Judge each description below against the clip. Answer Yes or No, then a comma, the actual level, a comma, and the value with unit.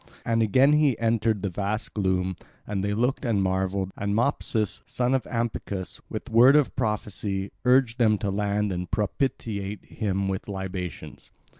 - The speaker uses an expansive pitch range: No, average, 3.2 semitones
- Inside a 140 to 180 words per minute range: Yes, average, 155 wpm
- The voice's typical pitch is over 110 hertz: No, low, 105 Hz